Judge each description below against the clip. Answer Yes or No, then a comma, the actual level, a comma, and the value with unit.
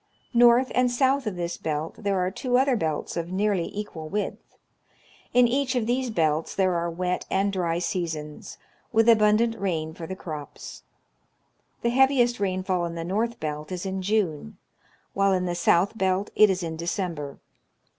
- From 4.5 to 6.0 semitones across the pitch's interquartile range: Yes, average, 4.9 semitones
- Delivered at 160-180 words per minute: Yes, average, 170 wpm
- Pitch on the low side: No, high, 190 Hz